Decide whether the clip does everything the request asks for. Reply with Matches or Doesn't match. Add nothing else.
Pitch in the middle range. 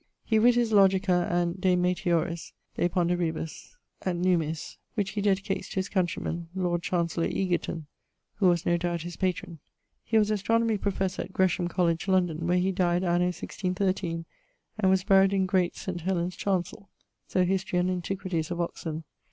Matches